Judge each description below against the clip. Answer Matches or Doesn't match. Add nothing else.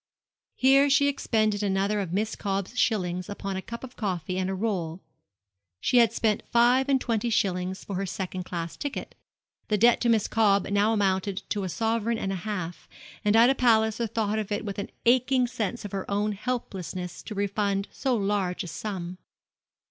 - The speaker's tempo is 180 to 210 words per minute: Matches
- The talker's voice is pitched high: Matches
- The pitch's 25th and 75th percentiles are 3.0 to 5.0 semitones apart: Matches